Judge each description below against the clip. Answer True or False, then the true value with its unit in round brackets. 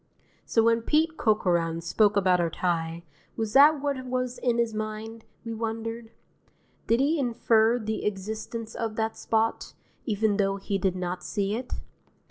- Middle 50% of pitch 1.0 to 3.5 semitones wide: True (2.9 semitones)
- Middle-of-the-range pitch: False (220 Hz)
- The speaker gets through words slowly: False (155 wpm)